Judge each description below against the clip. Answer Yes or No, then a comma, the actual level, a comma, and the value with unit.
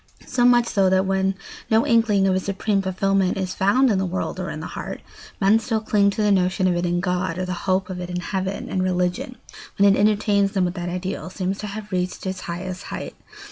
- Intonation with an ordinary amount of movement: No, narrow, 1.8 semitones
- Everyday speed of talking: No, fast, 235 wpm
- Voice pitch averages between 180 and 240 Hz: Yes, high, 190 Hz